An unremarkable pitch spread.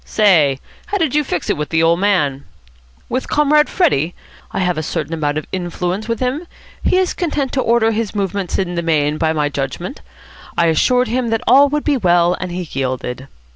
No: wide, 8.0 semitones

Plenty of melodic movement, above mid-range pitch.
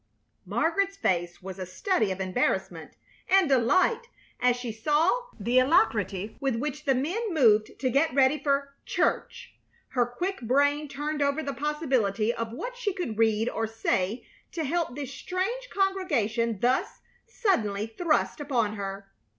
Yes: wide, 6.7 semitones; very high, 270 Hz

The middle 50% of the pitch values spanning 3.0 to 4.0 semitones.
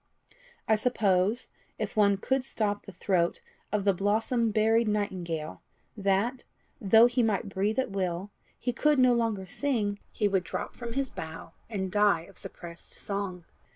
Yes: average, 3.3 semitones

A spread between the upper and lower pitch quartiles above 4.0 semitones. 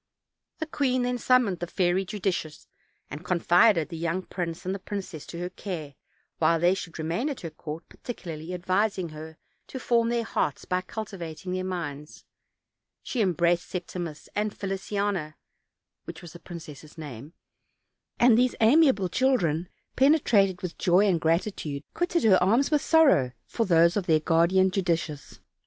Yes: average, 4.4 semitones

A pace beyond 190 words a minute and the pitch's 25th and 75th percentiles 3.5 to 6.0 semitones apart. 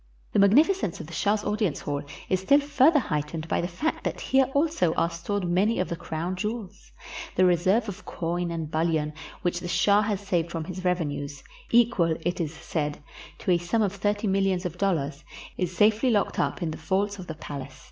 Yes: fast, 205 wpm; average, 3.9 semitones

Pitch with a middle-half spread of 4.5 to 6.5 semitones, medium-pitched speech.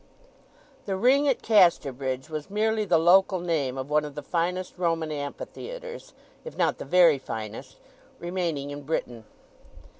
Yes: average, 5.1 semitones; medium, 165 Hz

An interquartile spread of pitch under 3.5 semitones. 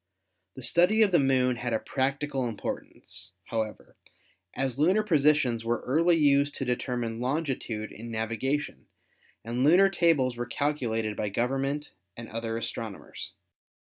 No: average, 4.2 semitones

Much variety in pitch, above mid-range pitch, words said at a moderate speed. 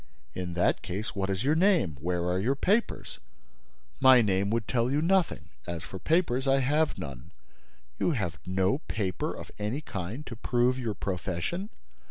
No: wide, 7.2 semitones; low, 115 Hz; average, 170 wpm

